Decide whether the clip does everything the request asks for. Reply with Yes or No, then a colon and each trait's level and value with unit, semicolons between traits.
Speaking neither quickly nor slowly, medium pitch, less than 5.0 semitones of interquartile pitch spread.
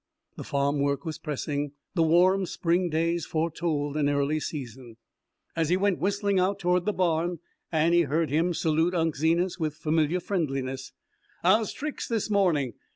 Yes: average, 160 wpm; medium, 165 Hz; average, 3.6 semitones